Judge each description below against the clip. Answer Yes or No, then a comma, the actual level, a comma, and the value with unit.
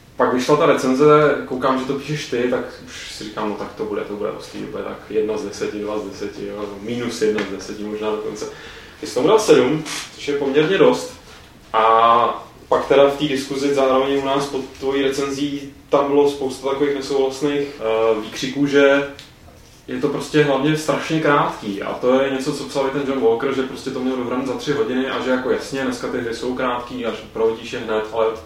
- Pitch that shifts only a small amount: No, average, 3.4 semitones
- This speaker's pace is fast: Yes, fast, 205 wpm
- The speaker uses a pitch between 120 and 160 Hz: Yes, low, 135 Hz